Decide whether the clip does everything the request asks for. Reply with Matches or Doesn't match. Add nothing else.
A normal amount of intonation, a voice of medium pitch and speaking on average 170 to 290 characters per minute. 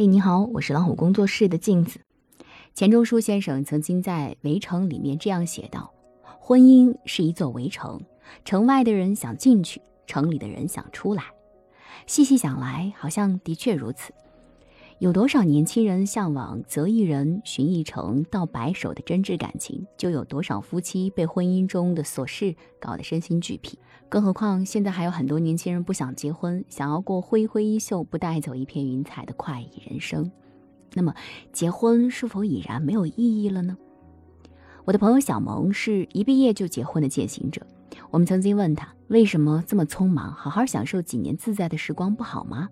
Doesn't match